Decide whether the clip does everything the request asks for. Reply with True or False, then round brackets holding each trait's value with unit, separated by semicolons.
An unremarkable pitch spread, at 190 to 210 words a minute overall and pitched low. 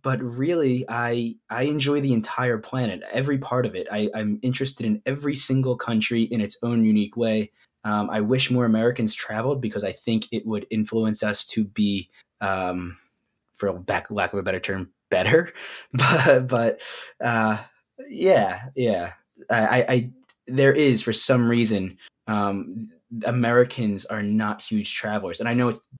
False (3.1 semitones; 165 wpm; 115 Hz)